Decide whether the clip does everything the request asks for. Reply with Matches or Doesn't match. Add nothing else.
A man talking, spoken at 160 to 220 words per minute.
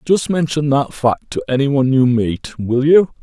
Matches